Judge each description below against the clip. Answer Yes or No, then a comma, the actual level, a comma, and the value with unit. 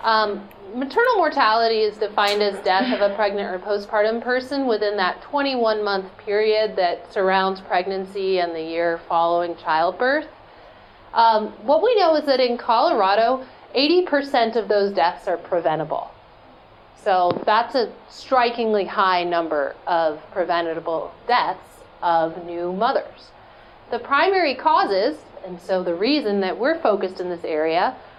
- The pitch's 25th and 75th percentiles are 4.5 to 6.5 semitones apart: Yes, average, 5.2 semitones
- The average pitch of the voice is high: Yes, high, 205 Hz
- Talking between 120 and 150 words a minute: Yes, average, 140 wpm